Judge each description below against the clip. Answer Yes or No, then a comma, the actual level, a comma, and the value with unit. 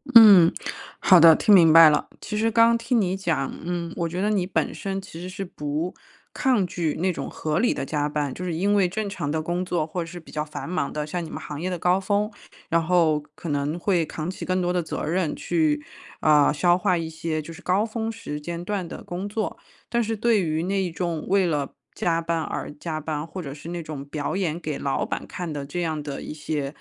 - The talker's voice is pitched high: No, medium, 170 Hz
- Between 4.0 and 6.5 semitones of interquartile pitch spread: No, average, 3.3 semitones